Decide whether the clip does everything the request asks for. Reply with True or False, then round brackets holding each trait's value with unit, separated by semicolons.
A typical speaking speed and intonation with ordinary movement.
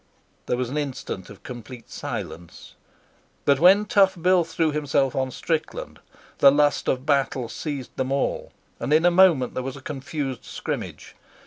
True (160 wpm; 3.9 semitones)